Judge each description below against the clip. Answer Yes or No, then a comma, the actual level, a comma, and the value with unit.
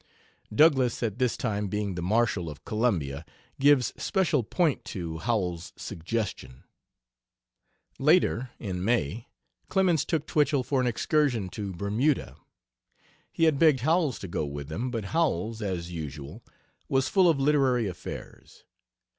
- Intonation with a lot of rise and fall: Yes, wide, 7.5 semitones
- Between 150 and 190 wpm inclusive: No, slow, 135 wpm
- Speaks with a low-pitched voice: Yes, low, 115 Hz